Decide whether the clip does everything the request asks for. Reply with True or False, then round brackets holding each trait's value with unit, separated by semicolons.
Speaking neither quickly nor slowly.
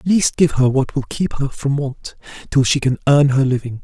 False (265 wpm)